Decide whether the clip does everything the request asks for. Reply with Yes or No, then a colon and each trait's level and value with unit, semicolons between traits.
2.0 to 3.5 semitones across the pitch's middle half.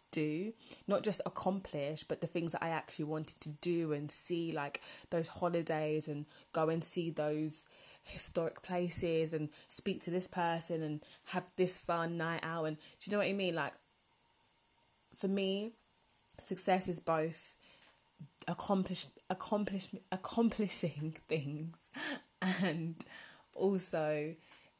Yes: average, 3.1 semitones